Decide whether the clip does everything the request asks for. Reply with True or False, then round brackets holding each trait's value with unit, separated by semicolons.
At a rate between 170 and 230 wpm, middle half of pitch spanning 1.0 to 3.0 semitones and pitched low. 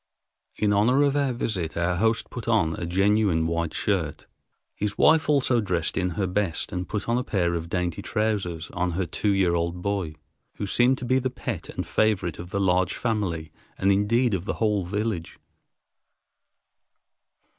False (175 wpm; 4.3 semitones; 100 Hz)